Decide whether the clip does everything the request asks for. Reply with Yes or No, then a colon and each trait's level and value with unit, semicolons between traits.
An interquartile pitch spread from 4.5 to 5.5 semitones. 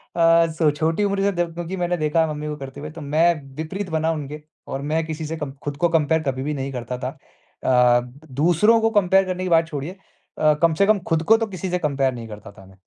No: average, 3.7 semitones